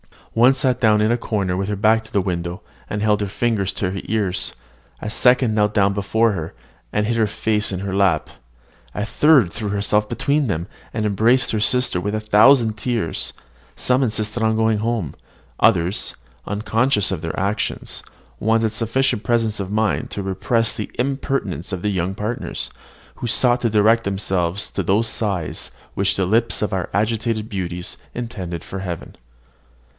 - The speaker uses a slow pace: No, average, 175 wpm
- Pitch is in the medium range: No, low, 105 Hz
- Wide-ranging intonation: No, average, 2.9 semitones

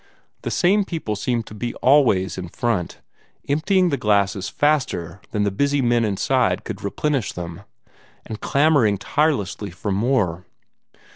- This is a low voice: Yes, low, 115 Hz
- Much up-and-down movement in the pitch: Yes, wide, 6.4 semitones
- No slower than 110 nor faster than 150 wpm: Yes, average, 140 wpm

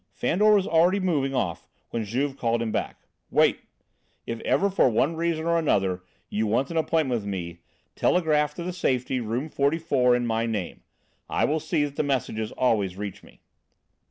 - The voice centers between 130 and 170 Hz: Yes, low, 135 Hz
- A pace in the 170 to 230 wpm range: Yes, average, 180 wpm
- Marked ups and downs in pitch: Yes, wide, 6.3 semitones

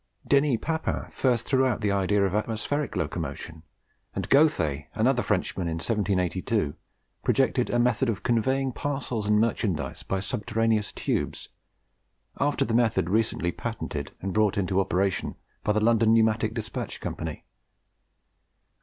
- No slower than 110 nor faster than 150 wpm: Yes, slow, 135 wpm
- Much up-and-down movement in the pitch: No, average, 3.7 semitones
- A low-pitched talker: Yes, low, 110 Hz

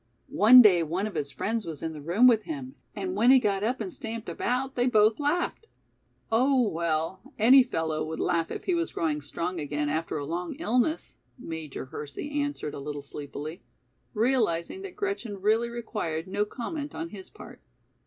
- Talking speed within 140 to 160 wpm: No, average, 185 wpm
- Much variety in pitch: Yes, wide, 7.7 semitones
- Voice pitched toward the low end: No, high, 210 Hz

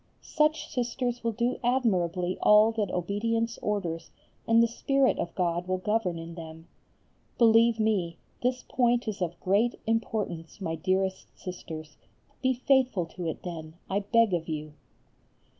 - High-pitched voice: Yes, high, 205 Hz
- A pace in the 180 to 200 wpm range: No, average, 145 wpm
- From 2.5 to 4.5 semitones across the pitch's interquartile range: No, average, 5.3 semitones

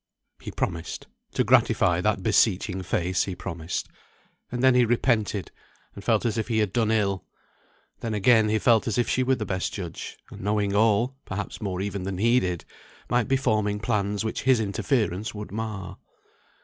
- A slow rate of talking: No, average, 180 wpm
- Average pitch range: Yes, average, 3.0 semitones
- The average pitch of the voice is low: Yes, low, 105 Hz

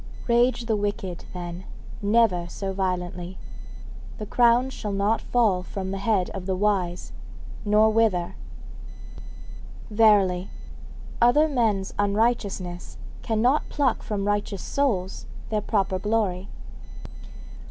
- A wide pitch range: No, average, 3.4 semitones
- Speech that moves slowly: Yes, slow, 110 wpm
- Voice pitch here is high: Yes, high, 205 Hz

